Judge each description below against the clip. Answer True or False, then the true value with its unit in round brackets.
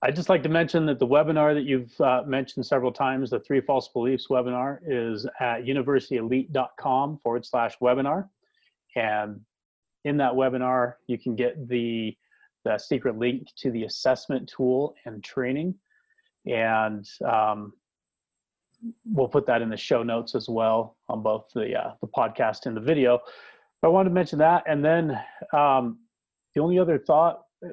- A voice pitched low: True (130 Hz)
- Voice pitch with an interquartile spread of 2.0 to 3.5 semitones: False (4.3 semitones)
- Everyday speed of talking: True (160 wpm)